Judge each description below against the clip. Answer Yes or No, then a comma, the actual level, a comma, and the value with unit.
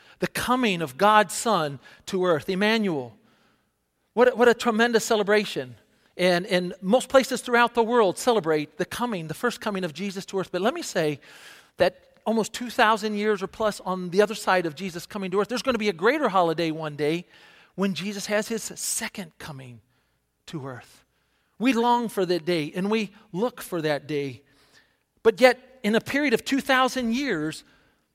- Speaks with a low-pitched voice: No, high, 200 Hz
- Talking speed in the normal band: Yes, average, 185 wpm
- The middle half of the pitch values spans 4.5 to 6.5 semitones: Yes, average, 5.0 semitones